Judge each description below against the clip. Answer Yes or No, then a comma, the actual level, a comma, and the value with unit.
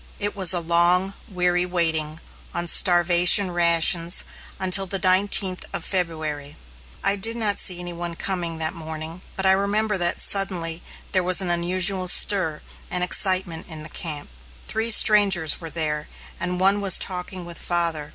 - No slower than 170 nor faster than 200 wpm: No, average, 160 wpm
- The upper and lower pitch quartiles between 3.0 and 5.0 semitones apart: No, narrow, 2.4 semitones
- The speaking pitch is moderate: Yes, medium, 180 Hz